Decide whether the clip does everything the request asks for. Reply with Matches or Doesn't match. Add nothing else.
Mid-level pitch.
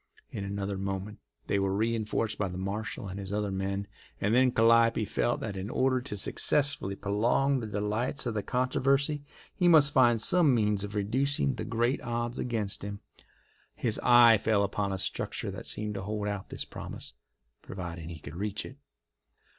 Doesn't match